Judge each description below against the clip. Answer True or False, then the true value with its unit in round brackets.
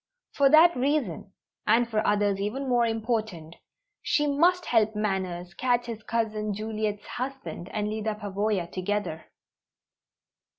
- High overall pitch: True (215 Hz)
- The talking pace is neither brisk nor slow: False (125 wpm)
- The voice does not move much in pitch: False (3.1 semitones)